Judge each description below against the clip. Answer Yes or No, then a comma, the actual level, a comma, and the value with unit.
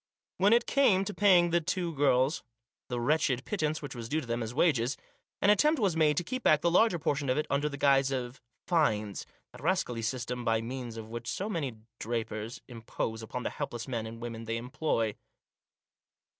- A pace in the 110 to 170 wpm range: No, average, 200 wpm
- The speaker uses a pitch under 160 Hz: Yes, low, 135 Hz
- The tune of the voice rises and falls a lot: Yes, wide, 6.0 semitones